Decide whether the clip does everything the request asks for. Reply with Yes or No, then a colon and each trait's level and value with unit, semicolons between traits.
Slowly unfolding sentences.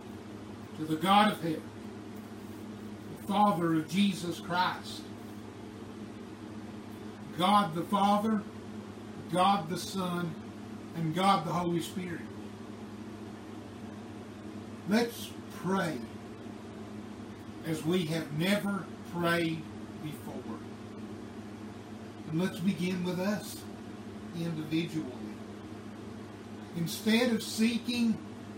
Yes: slow, 80 wpm